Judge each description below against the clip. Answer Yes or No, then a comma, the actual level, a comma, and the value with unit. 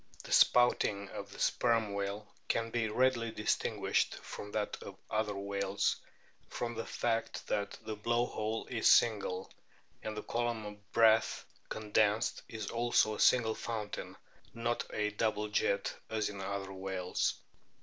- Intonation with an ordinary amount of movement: No, narrow, 2.2 semitones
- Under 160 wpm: Yes, average, 145 wpm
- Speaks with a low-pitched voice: Yes, low, 110 Hz